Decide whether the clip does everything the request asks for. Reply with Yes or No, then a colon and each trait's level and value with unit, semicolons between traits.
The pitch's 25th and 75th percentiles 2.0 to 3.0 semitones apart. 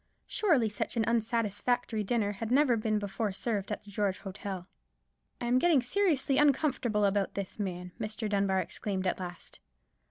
No: average, 3.5 semitones